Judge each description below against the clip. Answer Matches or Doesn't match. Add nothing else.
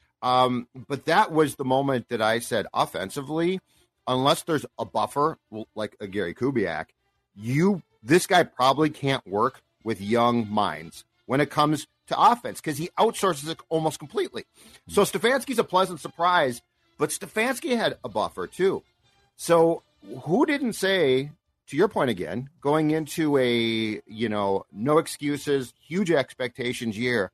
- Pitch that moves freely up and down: Matches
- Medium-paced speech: Matches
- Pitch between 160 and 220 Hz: Doesn't match